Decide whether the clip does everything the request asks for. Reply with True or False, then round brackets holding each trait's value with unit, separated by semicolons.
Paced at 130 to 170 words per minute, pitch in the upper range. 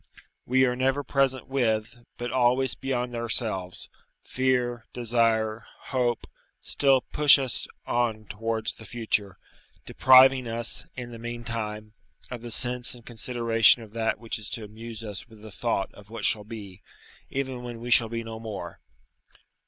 False (155 wpm; 115 Hz)